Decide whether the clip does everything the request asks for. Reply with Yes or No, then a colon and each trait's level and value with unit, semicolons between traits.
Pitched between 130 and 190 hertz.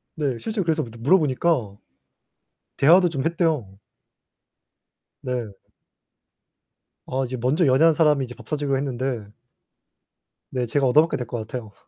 Yes: low, 135 Hz